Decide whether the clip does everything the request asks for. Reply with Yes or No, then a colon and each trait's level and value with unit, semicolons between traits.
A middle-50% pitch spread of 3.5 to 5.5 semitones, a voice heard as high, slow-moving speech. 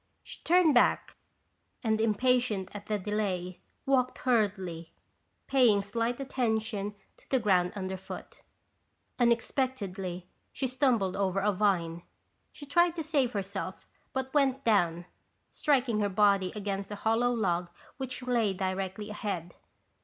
Yes: average, 4.7 semitones; high, 210 Hz; slow, 125 wpm